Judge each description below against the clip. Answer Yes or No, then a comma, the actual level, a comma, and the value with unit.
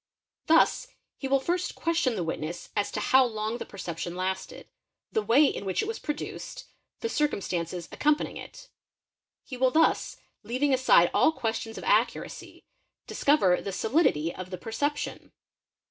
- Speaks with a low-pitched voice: No, high, 235 Hz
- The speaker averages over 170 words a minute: No, average, 155 wpm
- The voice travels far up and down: Yes, wide, 8.1 semitones